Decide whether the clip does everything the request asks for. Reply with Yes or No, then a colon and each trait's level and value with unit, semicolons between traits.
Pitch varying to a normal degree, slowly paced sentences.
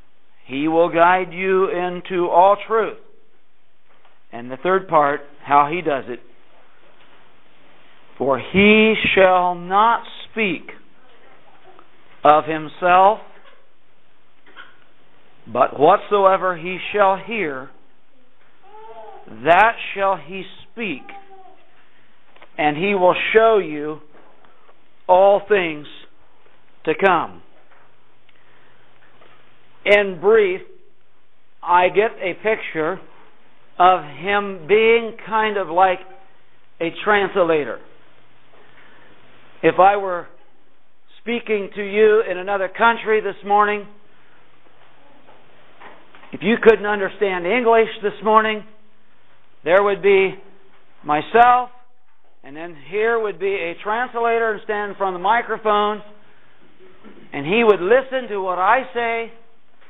Yes: average, 3.6 semitones; slow, 95 wpm